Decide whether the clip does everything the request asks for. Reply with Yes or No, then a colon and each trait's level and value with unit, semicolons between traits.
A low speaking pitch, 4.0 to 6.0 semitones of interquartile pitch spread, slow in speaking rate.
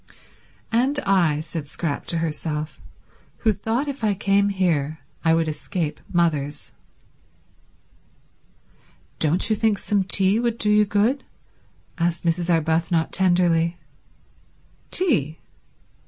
No: medium, 175 Hz; average, 4.4 semitones; slow, 110 wpm